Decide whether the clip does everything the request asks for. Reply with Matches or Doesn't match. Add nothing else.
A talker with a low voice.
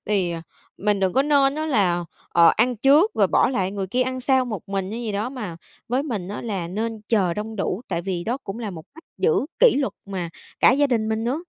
Doesn't match